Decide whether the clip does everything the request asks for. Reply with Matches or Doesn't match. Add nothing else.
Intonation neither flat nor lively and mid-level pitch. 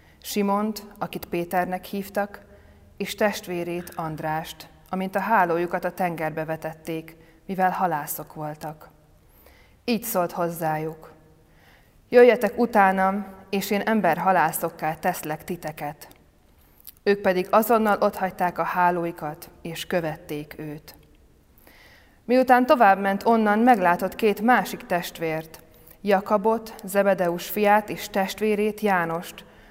Matches